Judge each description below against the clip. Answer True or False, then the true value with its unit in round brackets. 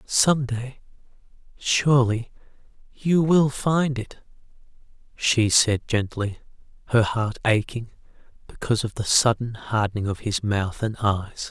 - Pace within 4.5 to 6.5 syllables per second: False (4.0 syllables/s)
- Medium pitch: False (115 Hz)